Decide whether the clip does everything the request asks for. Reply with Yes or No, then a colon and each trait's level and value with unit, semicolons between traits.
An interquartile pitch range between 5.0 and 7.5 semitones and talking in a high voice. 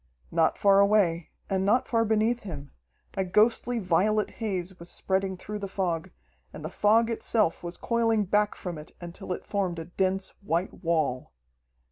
No: average, 3.5 semitones; high, 195 Hz